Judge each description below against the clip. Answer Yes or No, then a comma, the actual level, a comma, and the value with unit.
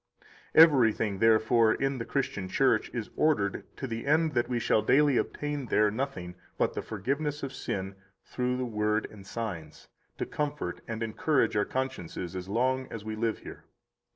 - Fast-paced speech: No, average, 175 wpm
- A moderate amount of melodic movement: Yes, average, 4.3 semitones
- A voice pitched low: Yes, low, 115 Hz